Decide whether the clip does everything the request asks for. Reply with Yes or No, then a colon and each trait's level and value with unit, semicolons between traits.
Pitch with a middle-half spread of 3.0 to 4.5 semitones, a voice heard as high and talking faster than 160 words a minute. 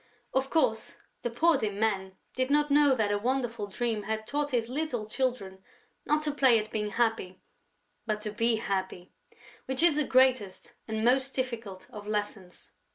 Yes: average, 4.0 semitones; high, 230 Hz; average, 170 wpm